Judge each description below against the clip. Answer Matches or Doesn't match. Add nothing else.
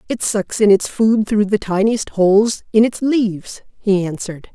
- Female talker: Matches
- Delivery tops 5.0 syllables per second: Doesn't match